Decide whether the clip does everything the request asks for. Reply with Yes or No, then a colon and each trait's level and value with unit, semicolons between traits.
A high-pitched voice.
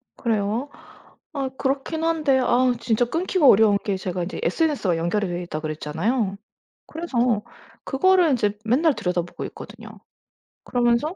Yes: high, 235 Hz